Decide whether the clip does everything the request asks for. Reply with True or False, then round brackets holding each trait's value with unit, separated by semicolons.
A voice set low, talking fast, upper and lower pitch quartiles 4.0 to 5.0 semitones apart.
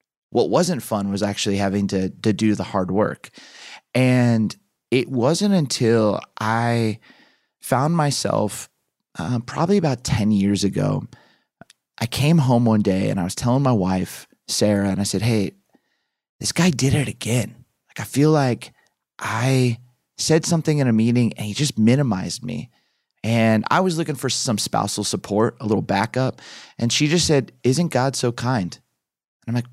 False (120 Hz; 170 wpm; 4.7 semitones)